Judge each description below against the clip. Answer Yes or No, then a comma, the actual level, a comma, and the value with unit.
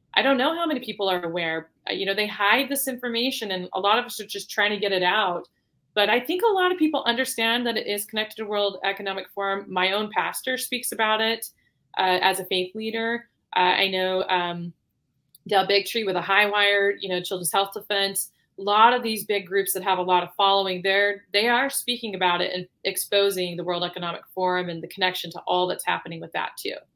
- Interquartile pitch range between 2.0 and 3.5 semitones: Yes, average, 3.2 semitones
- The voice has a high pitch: Yes, high, 200 Hz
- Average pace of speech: No, fast, 225 wpm